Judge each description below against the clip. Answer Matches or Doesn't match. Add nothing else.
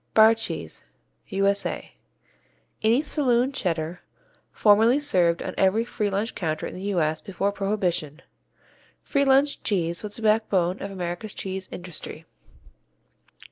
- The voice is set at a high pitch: Matches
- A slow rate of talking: Matches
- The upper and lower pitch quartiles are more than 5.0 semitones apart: Doesn't match